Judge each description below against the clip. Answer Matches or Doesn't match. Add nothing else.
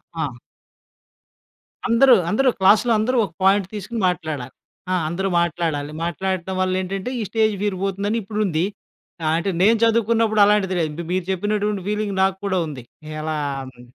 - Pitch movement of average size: Matches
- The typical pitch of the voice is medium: Doesn't match